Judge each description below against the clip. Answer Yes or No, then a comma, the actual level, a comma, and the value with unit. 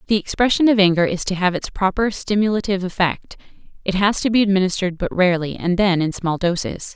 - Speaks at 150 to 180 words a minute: No, fast, 205 wpm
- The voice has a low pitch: No, high, 190 Hz